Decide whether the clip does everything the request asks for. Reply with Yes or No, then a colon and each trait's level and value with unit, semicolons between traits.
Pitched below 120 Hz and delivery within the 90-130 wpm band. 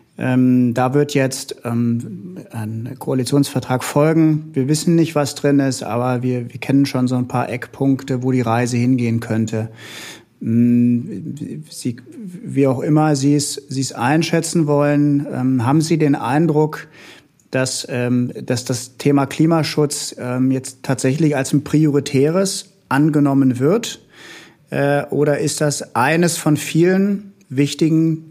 No: medium, 140 Hz; slow, 125 wpm